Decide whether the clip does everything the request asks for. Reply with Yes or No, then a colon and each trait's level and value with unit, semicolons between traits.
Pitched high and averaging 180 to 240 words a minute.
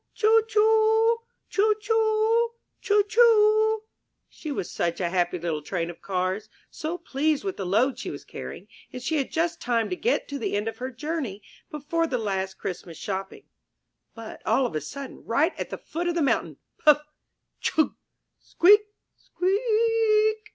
No: very high, 310 Hz; average, 170 wpm